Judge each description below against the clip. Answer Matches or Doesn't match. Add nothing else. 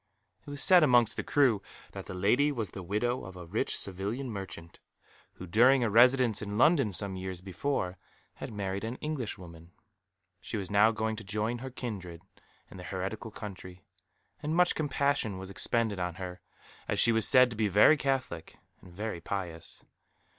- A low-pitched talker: Matches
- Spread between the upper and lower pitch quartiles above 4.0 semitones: Matches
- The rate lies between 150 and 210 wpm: Matches